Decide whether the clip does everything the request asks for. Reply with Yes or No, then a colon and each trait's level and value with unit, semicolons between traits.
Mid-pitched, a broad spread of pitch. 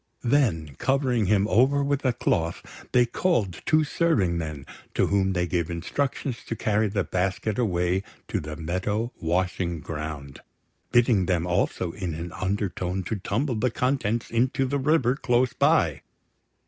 No: low, 100 Hz; wide, 6.2 semitones